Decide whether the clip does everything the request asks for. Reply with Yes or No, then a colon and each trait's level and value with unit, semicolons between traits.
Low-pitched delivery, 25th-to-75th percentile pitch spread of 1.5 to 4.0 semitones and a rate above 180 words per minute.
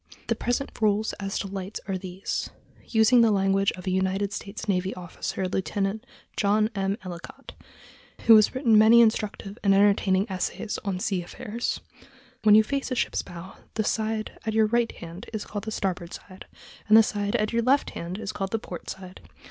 No: high, 205 Hz; narrow, 2.4 semitones; average, 190 wpm